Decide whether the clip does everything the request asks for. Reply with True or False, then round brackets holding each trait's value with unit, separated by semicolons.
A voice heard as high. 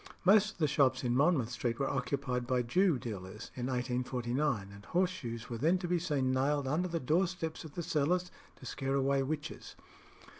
False (135 Hz)